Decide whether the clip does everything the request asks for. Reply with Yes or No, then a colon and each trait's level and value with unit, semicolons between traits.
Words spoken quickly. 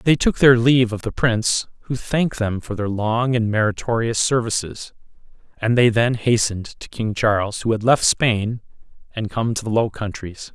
No: average, 190 wpm